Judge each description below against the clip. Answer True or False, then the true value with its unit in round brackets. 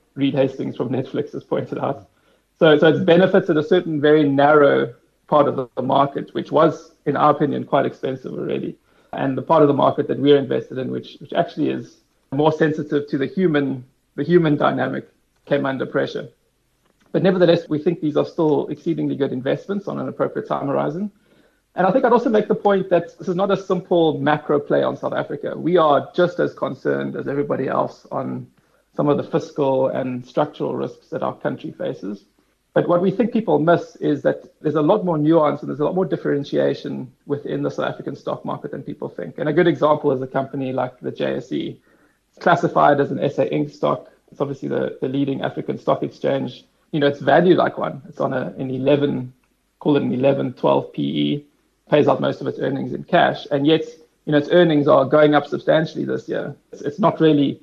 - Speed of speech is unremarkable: False (210 wpm)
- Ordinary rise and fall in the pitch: True (3.8 semitones)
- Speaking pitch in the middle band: True (150 Hz)